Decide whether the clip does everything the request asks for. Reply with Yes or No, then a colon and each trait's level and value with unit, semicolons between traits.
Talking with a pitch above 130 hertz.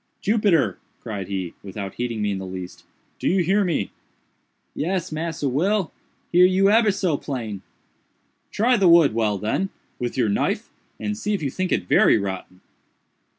Yes: medium, 140 Hz